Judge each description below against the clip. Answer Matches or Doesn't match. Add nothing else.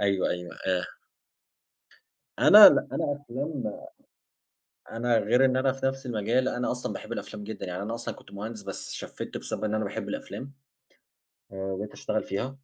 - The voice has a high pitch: Doesn't match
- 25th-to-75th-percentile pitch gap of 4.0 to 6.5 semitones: Matches